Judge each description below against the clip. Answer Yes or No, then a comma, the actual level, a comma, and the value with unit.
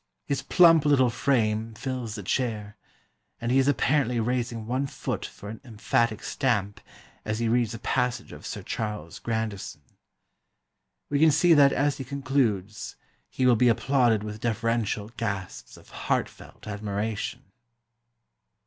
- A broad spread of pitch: No, average, 3.7 semitones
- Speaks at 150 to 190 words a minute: No, average, 140 wpm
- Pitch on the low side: Yes, low, 115 Hz